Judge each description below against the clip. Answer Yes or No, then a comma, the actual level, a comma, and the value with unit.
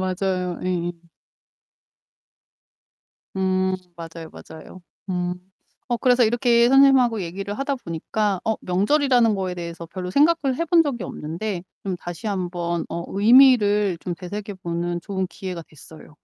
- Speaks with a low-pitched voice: No, high, 190 Hz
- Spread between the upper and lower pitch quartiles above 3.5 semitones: Yes, average, 5.2 semitones